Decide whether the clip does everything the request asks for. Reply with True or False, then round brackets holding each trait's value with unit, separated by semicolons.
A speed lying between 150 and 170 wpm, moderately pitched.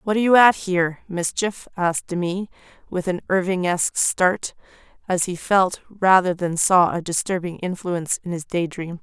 True (165 wpm; 180 Hz)